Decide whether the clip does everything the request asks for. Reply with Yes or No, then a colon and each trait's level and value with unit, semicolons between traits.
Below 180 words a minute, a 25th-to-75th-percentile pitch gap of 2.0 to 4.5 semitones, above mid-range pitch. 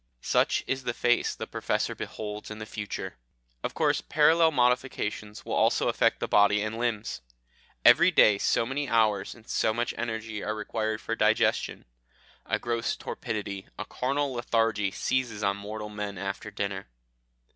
No: average, 155 wpm; narrow, 2.5 semitones; low, 110 Hz